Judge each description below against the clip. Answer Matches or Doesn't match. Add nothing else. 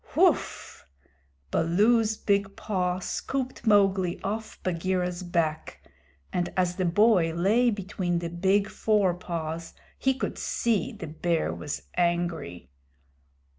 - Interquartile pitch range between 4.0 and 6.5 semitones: Doesn't match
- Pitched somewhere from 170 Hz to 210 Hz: Matches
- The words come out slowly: Matches